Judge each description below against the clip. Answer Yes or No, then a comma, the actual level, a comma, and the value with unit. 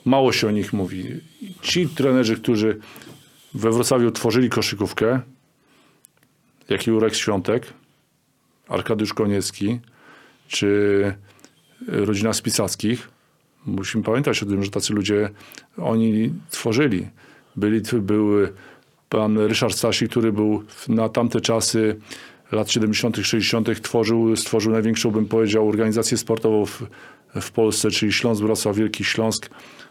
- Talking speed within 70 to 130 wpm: Yes, slow, 110 wpm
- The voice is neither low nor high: No, low, 110 Hz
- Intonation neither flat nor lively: No, narrow, 2.1 semitones